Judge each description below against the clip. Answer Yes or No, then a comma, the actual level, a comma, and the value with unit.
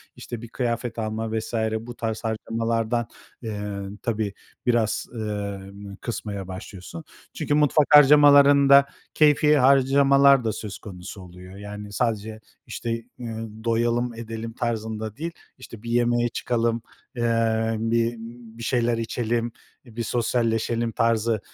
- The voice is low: Yes, low, 115 Hz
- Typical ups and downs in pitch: No, narrow, 1.8 semitones